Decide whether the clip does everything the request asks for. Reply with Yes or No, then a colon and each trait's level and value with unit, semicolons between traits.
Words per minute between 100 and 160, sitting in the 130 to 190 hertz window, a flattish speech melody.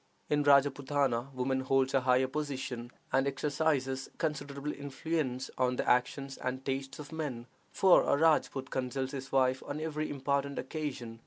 Yes: average, 150 wpm; low, 135 Hz; narrow, 1.8 semitones